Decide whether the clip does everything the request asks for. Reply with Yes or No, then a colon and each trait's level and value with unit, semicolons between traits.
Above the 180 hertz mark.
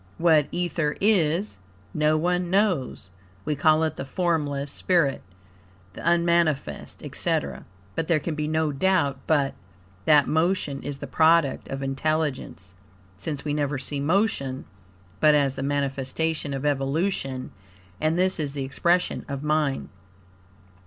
No: medium, 150 Hz